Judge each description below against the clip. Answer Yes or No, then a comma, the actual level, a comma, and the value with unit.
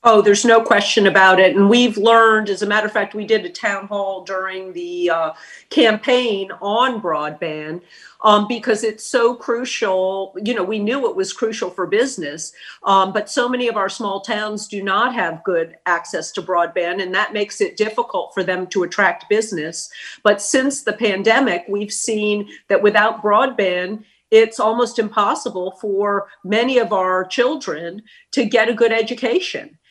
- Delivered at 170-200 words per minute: Yes, average, 175 wpm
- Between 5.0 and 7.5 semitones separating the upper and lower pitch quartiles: No, average, 3.4 semitones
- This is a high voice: Yes, high, 210 Hz